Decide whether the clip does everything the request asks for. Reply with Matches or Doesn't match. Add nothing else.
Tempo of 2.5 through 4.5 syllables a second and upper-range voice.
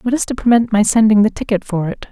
Doesn't match